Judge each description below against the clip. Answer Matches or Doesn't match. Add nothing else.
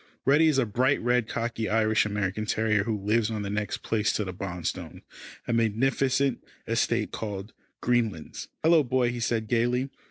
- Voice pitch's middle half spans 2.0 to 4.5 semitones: Matches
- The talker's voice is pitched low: Matches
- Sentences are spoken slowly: Doesn't match